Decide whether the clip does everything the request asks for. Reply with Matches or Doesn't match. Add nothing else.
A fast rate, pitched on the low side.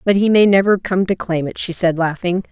Doesn't match